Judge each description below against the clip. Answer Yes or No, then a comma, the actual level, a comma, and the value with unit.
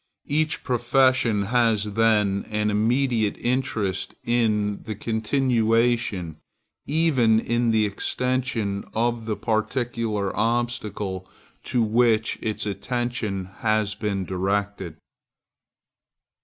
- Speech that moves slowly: Yes, slow, 90 wpm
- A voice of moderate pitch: No, low, 110 Hz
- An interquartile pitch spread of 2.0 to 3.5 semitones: Yes, average, 2.8 semitones